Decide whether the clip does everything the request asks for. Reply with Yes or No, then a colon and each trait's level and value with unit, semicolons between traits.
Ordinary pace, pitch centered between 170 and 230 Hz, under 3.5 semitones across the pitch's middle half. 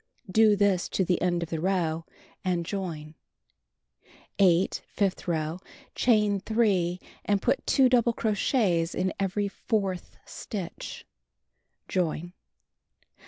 No: slow, 115 wpm; high, 190 Hz; average, 3.1 semitones